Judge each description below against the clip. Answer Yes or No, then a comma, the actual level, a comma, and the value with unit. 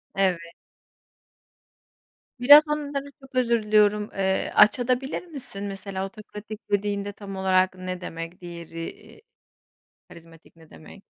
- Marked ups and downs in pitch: No, average, 4.3 semitones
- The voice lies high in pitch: Yes, high, 200 Hz